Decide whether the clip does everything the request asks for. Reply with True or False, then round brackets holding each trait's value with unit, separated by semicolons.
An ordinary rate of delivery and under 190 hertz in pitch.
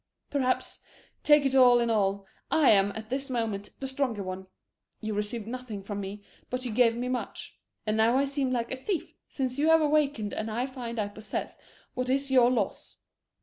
False (190 wpm; 245 Hz)